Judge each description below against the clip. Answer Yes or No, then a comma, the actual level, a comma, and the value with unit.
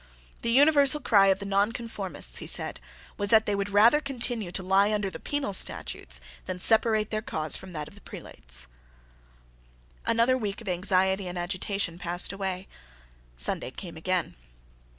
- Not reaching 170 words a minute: Yes, average, 160 wpm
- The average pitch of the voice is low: No, high, 200 Hz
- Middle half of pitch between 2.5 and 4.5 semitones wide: Yes, average, 3.5 semitones